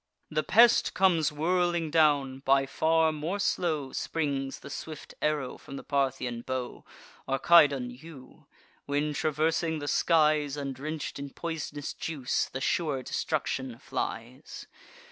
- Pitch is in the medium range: Yes, medium, 145 Hz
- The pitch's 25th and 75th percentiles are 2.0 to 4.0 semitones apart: Yes, average, 3.1 semitones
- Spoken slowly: Yes, slow, 130 wpm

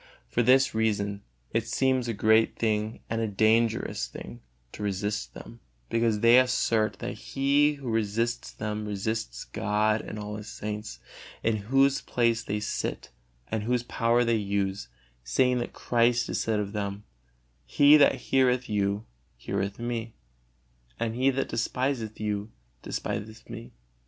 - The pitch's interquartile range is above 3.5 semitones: No, narrow, 2.5 semitones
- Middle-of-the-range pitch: No, low, 110 Hz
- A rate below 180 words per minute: Yes, average, 140 wpm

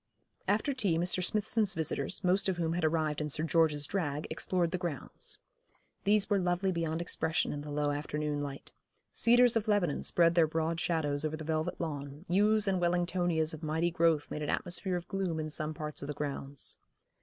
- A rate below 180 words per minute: No, average, 190 wpm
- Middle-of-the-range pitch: Yes, medium, 165 Hz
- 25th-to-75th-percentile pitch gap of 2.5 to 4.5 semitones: Yes, average, 3.2 semitones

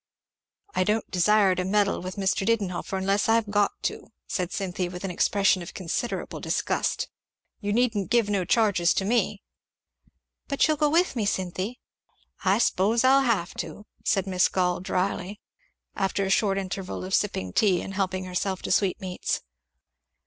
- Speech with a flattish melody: Yes, narrow, 2.3 semitones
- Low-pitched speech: No, high, 195 Hz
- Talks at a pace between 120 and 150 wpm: No, average, 160 wpm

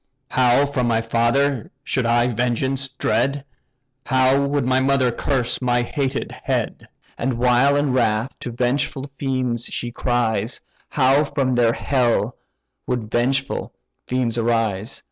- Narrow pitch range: Yes, narrow, 2.3 semitones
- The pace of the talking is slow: Yes, slow, 130 wpm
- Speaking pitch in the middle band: No, low, 125 Hz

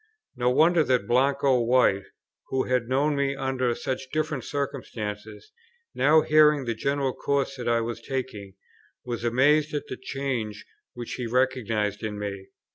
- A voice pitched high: No, low, 130 Hz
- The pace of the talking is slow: No, average, 150 wpm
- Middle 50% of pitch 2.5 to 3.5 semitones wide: Yes, average, 3.0 semitones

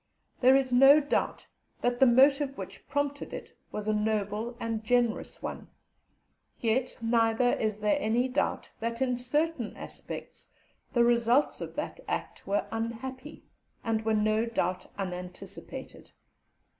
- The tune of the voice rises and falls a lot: No, average, 3.1 semitones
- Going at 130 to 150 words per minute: Yes, slow, 135 wpm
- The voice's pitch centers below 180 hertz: No, high, 235 Hz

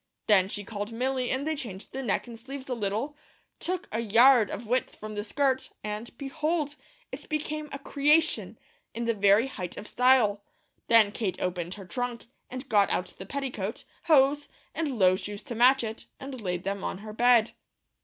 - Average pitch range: Yes, average, 4.7 semitones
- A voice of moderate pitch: No, high, 235 Hz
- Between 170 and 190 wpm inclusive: Yes, average, 185 wpm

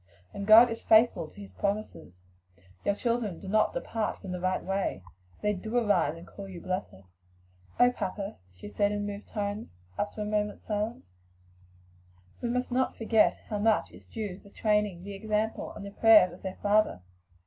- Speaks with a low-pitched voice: No, high, 205 Hz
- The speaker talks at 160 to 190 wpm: Yes, average, 180 wpm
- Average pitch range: No, narrow, 2.2 semitones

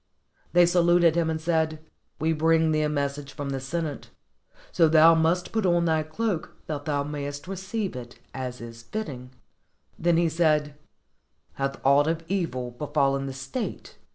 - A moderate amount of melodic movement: Yes, average, 3.3 semitones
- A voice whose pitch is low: No, medium, 155 Hz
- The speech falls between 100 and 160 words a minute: No, average, 170 wpm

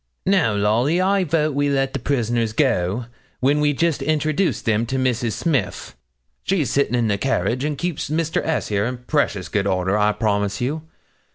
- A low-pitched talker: Yes, low, 130 Hz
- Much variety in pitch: Yes, wide, 5.9 semitones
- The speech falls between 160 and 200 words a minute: Yes, average, 180 wpm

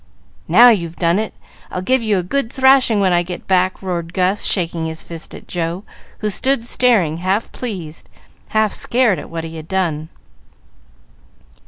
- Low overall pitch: No, medium, 185 Hz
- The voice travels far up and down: No, average, 4.7 semitones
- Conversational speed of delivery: Yes, average, 170 wpm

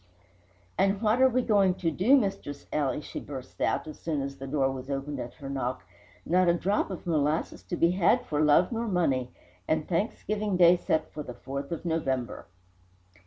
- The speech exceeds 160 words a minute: Yes, average, 195 wpm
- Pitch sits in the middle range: Yes, medium, 160 Hz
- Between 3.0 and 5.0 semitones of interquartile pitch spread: No, wide, 5.5 semitones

